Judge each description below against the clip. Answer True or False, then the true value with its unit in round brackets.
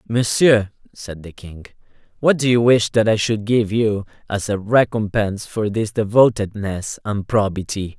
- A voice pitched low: True (105 Hz)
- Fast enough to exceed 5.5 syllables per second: False (4.4 syllables/s)